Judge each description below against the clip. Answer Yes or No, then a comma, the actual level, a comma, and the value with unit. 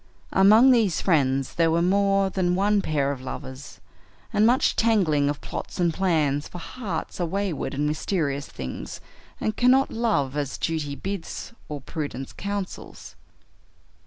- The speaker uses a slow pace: No, average, 145 wpm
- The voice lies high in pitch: No, medium, 170 Hz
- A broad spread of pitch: Yes, wide, 5.7 semitones